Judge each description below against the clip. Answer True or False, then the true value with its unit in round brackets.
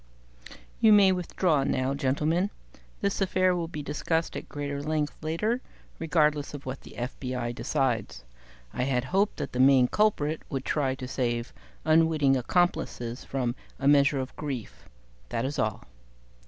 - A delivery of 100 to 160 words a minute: True (150 wpm)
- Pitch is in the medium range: True (145 Hz)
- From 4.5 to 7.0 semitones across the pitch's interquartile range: False (4.1 semitones)